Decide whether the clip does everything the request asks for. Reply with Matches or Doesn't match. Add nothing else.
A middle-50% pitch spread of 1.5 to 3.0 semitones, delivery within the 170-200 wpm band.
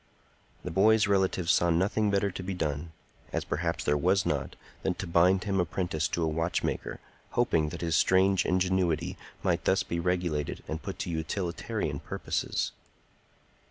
Doesn't match